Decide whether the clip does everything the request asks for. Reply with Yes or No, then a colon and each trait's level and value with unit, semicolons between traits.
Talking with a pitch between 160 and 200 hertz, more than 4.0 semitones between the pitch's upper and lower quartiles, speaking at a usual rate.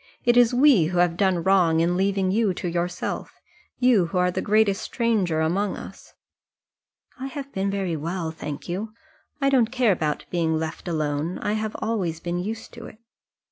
Yes: high, 190 Hz; average, 4.5 semitones; average, 180 wpm